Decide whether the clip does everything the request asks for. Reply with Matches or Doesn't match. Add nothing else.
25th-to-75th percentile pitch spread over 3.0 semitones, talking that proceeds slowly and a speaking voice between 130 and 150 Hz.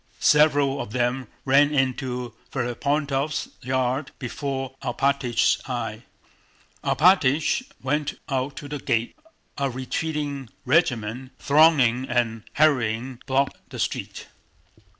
Doesn't match